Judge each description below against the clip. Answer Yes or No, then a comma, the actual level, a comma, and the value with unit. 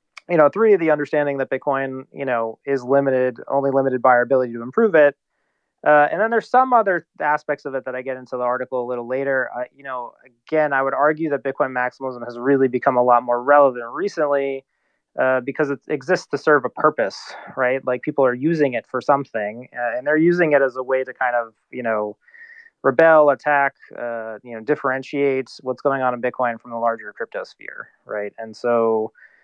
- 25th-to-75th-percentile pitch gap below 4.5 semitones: Yes, average, 2.9 semitones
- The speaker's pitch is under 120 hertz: No, low, 135 Hz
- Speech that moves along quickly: Yes, fast, 210 wpm